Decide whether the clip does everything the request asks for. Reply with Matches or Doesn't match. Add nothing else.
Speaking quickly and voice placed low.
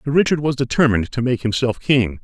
Matches